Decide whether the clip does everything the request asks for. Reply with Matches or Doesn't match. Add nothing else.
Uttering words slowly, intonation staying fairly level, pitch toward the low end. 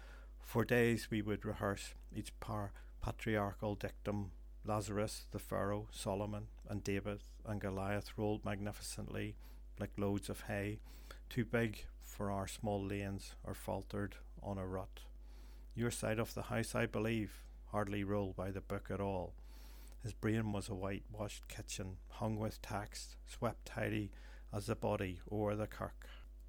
Doesn't match